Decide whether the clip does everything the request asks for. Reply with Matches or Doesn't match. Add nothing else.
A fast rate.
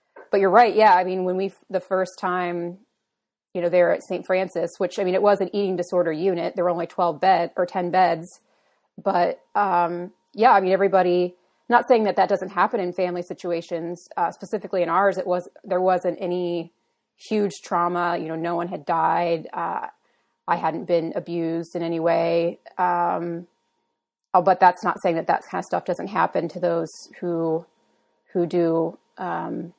Doesn't match